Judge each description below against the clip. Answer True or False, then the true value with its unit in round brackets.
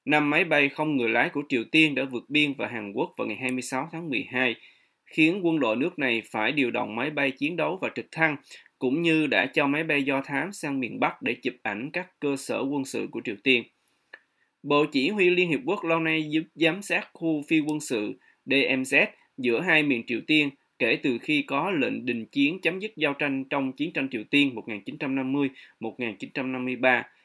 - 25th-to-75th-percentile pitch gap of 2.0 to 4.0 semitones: True (3.4 semitones)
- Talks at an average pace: True (210 wpm)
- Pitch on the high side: False (145 Hz)